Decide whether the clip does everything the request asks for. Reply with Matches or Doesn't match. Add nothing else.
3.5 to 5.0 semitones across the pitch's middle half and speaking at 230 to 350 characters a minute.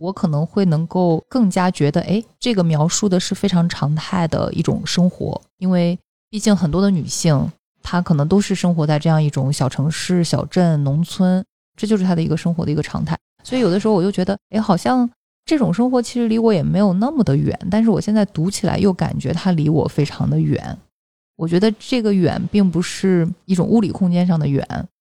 Matches